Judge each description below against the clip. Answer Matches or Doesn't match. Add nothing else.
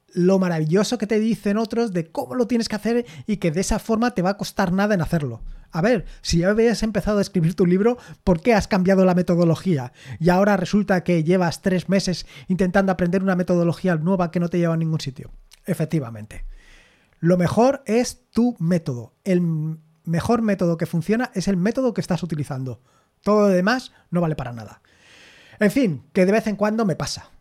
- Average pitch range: Matches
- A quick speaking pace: Matches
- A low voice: Doesn't match